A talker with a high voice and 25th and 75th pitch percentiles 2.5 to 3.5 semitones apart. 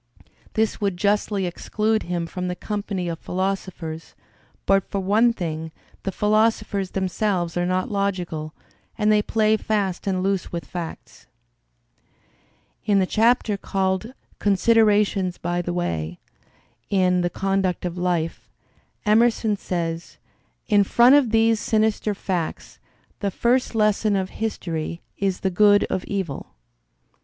Yes: high, 195 Hz; average, 3.2 semitones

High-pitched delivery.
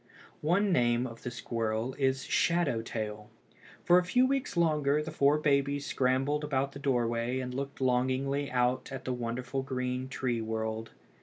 No: low, 130 Hz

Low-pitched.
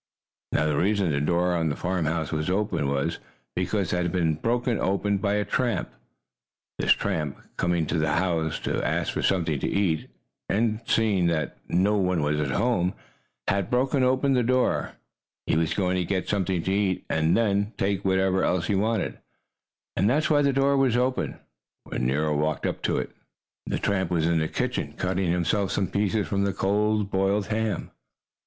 Yes: very low, 95 Hz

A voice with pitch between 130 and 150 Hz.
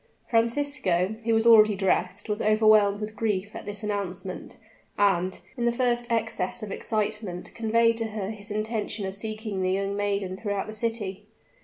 No: high, 210 Hz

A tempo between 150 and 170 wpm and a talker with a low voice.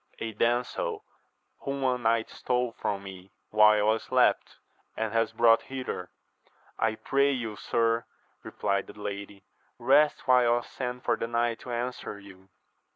Yes: average, 155 wpm; low, 115 Hz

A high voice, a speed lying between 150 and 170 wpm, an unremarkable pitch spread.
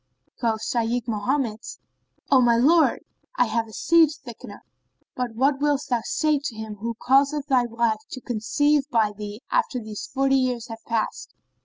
Yes: high, 245 Hz; average, 165 wpm; average, 3.5 semitones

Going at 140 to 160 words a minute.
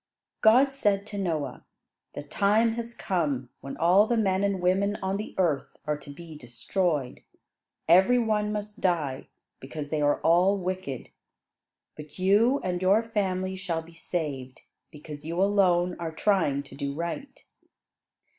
Yes: average, 150 wpm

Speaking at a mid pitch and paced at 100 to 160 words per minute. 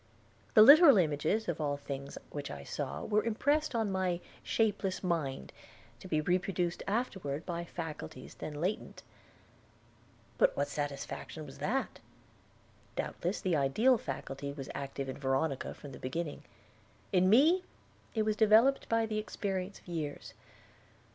Yes: medium, 180 Hz; average, 140 wpm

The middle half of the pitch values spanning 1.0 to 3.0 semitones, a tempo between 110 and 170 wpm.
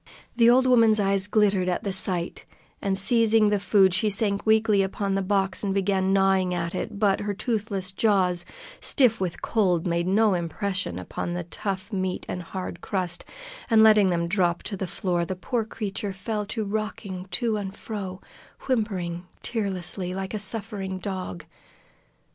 Yes: narrow, 2.5 semitones; average, 165 wpm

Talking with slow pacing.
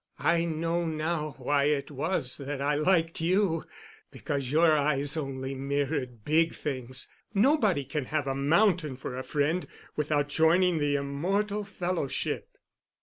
Yes: slow, 130 wpm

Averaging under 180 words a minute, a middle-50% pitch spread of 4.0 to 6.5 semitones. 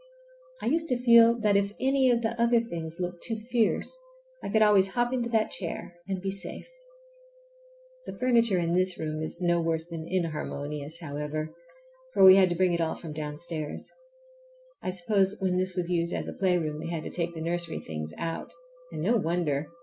No: average, 195 wpm; average, 4.4 semitones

